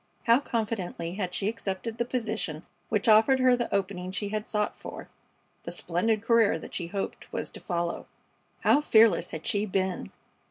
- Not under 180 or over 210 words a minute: No, average, 170 wpm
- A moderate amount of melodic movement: Yes, average, 3.5 semitones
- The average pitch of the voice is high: Yes, high, 210 Hz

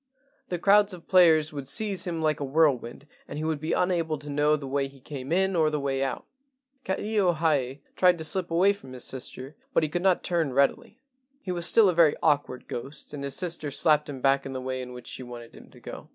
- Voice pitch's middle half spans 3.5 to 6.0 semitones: Yes, average, 4.2 semitones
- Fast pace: Yes, fast, 245 wpm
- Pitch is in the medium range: Yes, medium, 150 Hz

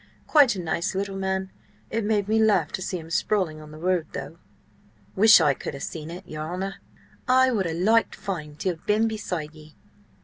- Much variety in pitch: No, average, 4.7 semitones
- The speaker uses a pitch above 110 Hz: Yes, medium, 185 Hz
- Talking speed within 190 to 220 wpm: Yes, fast, 205 wpm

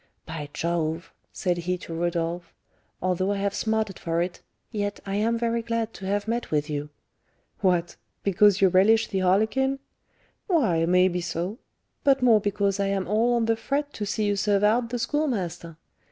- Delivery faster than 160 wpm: Yes, average, 180 wpm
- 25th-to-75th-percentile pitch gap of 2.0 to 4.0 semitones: No, average, 4.4 semitones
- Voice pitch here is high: Yes, high, 200 Hz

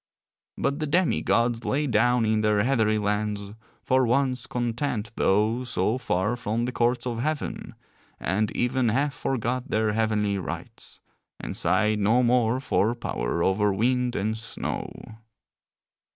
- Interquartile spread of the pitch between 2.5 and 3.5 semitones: Yes, average, 3.0 semitones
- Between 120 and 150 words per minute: Yes, average, 140 wpm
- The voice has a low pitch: Yes, low, 115 Hz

